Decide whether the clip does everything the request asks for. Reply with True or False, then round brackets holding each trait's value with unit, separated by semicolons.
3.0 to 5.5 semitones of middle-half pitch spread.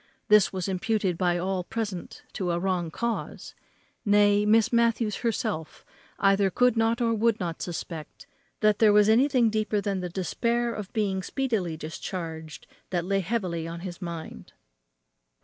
True (4.1 semitones)